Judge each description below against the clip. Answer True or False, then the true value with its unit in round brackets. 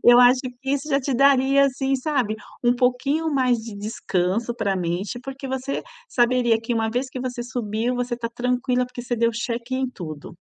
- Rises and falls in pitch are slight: True (2.3 semitones)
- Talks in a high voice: True (245 Hz)